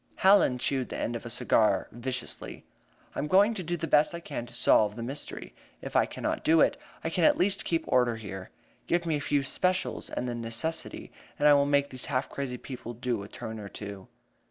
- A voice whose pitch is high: No, low, 135 Hz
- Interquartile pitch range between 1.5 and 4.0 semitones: No, wide, 5.6 semitones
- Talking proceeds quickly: Yes, fast, 225 wpm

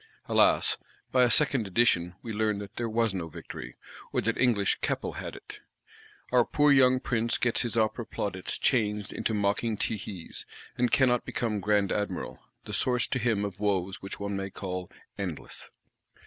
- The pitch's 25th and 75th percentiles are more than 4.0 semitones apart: No, average, 3.3 semitones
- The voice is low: Yes, low, 105 Hz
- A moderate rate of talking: Yes, average, 165 wpm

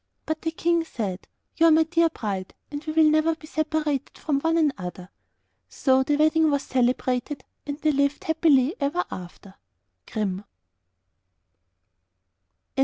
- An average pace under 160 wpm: Yes, average, 140 wpm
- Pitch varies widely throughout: No, average, 3.8 semitones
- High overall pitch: Yes, very high, 295 Hz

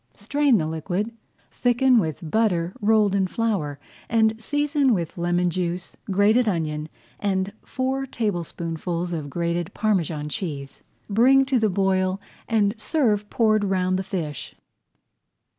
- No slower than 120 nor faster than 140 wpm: Yes, slow, 135 wpm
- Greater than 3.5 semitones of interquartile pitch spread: Yes, average, 4.7 semitones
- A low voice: No, high, 195 Hz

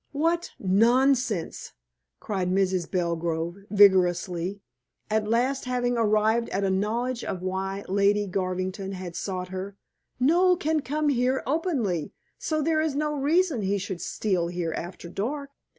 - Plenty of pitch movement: Yes, wide, 6.2 semitones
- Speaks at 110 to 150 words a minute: Yes, slow, 135 wpm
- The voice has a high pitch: Yes, high, 205 Hz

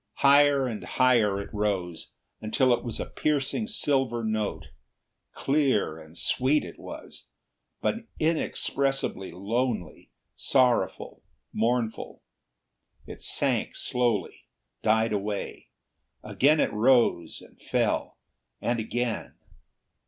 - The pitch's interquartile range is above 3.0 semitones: Yes, average, 4.4 semitones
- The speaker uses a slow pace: Yes, slow, 100 wpm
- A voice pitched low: Yes, low, 120 Hz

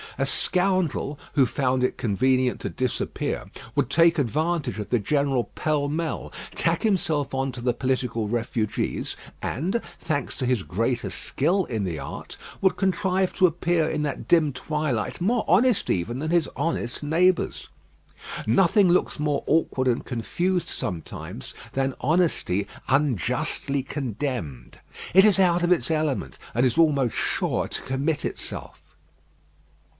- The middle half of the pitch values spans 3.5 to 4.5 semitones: No, wide, 5.5 semitones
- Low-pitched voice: No, medium, 145 Hz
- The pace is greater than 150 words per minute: No, average, 140 wpm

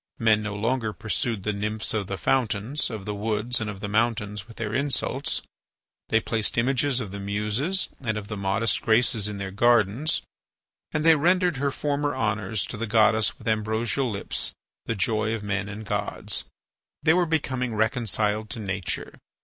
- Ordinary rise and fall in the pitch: Yes, average, 3.1 semitones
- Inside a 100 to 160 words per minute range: No, average, 175 wpm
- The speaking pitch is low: Yes, low, 110 Hz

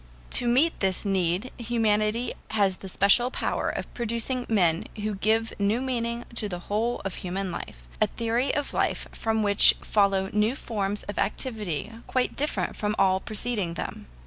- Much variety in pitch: No, average, 3.3 semitones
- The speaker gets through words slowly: No, average, 170 wpm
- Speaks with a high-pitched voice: Yes, high, 215 Hz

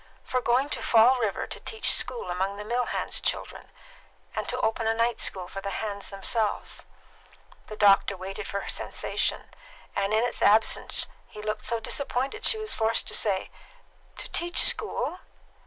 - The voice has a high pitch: Yes, high, 220 Hz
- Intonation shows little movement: No, average, 3.6 semitones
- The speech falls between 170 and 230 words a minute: Yes, average, 175 wpm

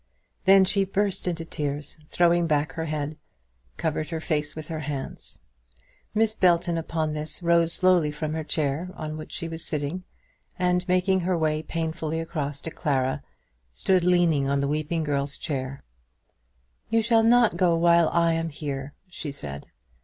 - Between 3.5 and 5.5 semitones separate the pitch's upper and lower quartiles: No, average, 2.8 semitones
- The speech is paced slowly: No, average, 165 wpm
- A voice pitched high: No, medium, 160 Hz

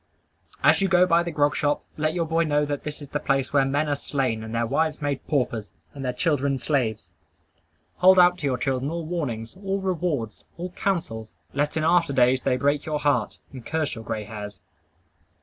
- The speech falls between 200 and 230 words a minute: Yes, fast, 205 wpm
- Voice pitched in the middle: Yes, medium, 145 Hz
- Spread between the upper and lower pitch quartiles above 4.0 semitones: Yes, average, 4.4 semitones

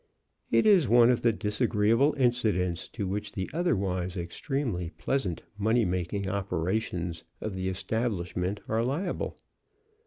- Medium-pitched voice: No, low, 105 Hz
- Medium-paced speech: No, slow, 125 wpm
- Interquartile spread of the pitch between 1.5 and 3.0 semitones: No, average, 4.7 semitones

